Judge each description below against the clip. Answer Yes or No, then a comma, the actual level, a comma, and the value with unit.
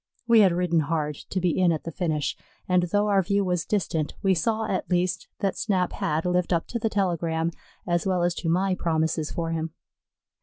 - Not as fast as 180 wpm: No, fast, 205 wpm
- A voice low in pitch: No, medium, 175 Hz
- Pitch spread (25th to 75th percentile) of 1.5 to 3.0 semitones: Yes, average, 2.7 semitones